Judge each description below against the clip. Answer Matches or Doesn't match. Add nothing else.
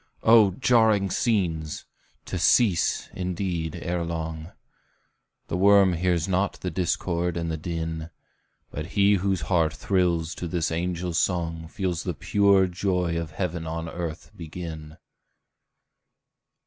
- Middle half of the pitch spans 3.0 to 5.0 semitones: Doesn't match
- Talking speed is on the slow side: Matches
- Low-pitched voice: Matches